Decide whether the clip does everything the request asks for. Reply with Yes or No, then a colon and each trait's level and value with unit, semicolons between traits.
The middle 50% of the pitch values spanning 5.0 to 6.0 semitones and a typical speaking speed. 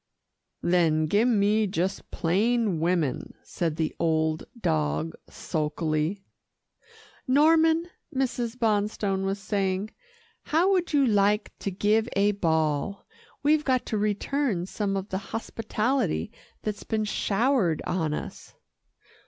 No: wide, 5.4 semitones; slow, 115 wpm